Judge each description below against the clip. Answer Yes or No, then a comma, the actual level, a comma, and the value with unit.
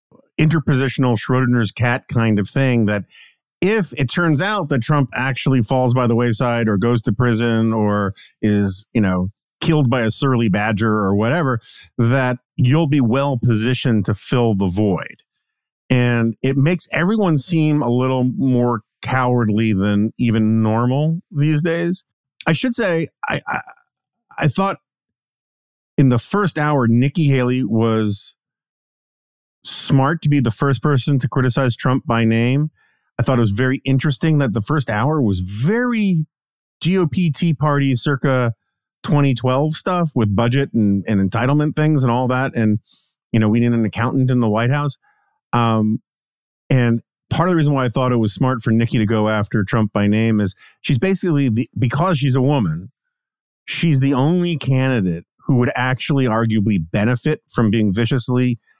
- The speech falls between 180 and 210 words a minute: No, average, 160 wpm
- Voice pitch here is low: Yes, low, 130 Hz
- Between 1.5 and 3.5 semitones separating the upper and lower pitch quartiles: No, average, 4.4 semitones